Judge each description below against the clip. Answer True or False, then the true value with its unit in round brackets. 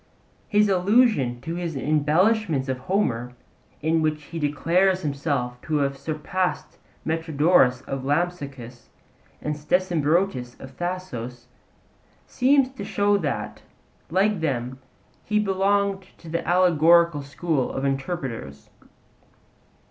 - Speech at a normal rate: False (110 wpm)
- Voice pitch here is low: False (160 Hz)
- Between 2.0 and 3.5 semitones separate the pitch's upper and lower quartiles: False (5.4 semitones)